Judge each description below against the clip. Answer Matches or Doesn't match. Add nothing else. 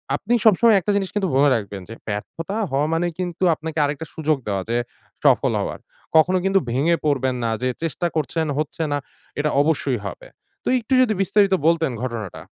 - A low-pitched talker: Doesn't match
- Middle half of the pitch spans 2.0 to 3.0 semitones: Doesn't match